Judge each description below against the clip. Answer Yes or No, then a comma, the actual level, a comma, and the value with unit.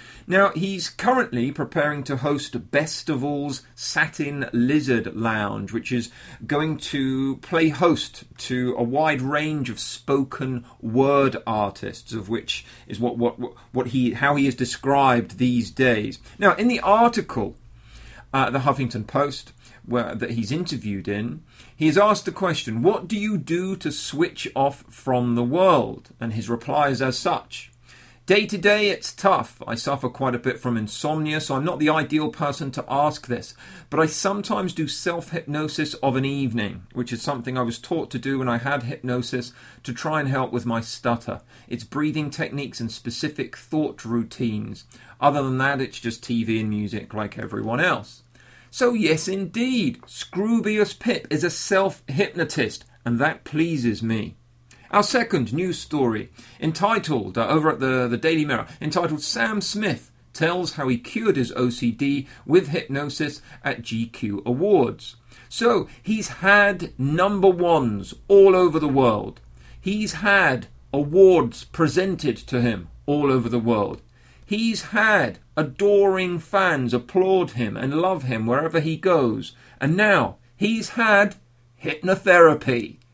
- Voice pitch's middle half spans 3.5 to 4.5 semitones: No, wide, 5.6 semitones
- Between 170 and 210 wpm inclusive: No, average, 155 wpm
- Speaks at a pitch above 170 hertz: No, medium, 140 Hz